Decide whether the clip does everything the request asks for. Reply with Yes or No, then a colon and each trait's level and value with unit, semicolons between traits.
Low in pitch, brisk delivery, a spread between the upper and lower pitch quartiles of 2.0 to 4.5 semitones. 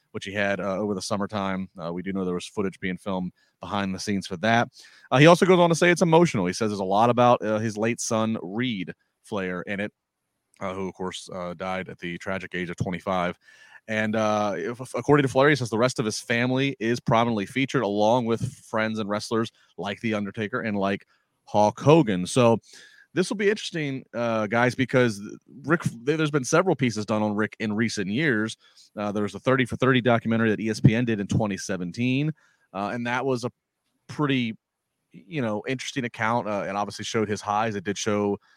Yes: low, 110 Hz; fast, 210 wpm; average, 3.9 semitones